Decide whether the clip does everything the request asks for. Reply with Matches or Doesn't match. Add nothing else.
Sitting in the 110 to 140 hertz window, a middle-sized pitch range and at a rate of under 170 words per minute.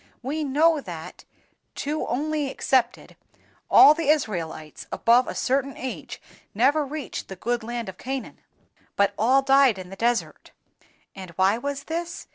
Doesn't match